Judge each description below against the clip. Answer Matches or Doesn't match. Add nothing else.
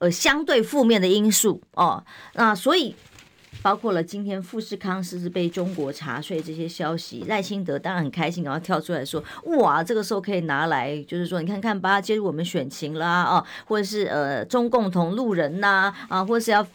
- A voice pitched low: Doesn't match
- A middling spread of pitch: Matches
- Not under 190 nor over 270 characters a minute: Doesn't match